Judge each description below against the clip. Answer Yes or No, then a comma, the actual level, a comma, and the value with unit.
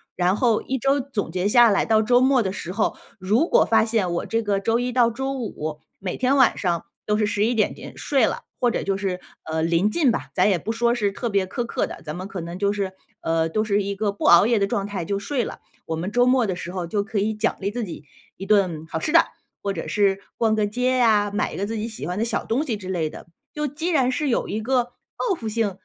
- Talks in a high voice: Yes, high, 210 Hz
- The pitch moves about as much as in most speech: Yes, average, 3.8 semitones